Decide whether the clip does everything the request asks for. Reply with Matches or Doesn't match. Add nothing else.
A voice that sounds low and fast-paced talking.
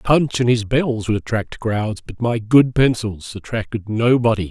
Doesn't match